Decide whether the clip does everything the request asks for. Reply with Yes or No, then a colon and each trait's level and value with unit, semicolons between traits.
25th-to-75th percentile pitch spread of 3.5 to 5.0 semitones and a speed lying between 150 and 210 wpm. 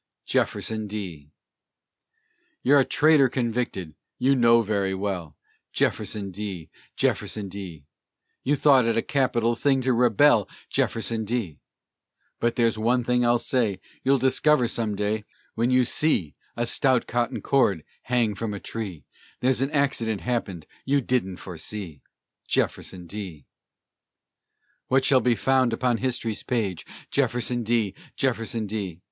No: average, 4.0 semitones; slow, 135 wpm